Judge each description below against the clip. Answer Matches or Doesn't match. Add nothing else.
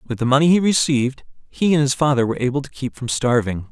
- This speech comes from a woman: Doesn't match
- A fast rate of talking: Matches